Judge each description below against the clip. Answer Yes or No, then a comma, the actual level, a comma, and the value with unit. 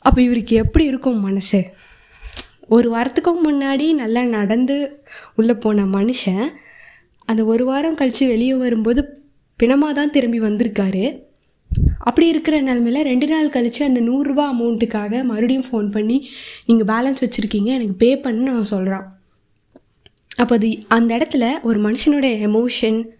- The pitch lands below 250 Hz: Yes, high, 240 Hz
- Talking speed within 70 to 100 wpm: No, fast, 130 wpm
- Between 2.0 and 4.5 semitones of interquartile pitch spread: Yes, average, 3.4 semitones